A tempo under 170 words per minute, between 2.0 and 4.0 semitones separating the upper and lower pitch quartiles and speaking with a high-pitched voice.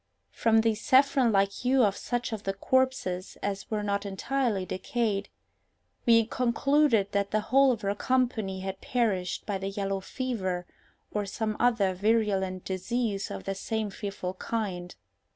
Yes: average, 150 wpm; average, 3.5 semitones; high, 210 Hz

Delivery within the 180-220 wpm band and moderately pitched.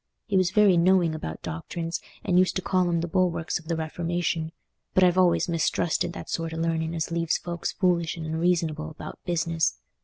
Yes: average, 190 wpm; medium, 170 Hz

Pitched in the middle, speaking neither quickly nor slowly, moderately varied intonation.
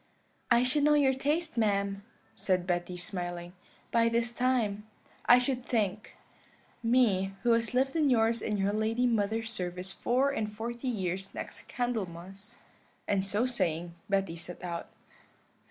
No: high, 220 Hz; average, 145 wpm; average, 4.3 semitones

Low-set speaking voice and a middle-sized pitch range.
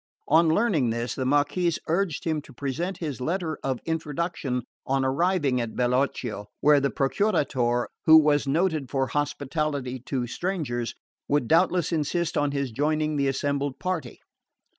No: medium, 145 Hz; average, 3.6 semitones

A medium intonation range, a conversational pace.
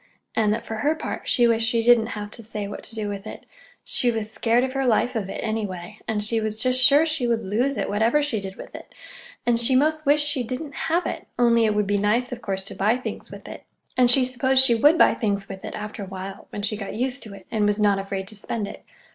No: average, 3.5 semitones; fast, 265 wpm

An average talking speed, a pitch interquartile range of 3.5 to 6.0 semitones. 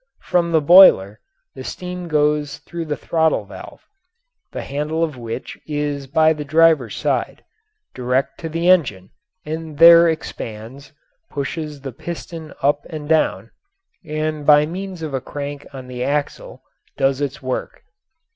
No: average, 145 wpm; average, 2.8 semitones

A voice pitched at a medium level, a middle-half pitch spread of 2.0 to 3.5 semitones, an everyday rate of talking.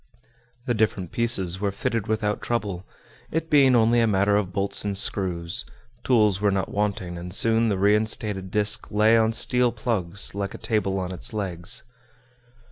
No: low, 105 Hz; average, 2.8 semitones; average, 165 wpm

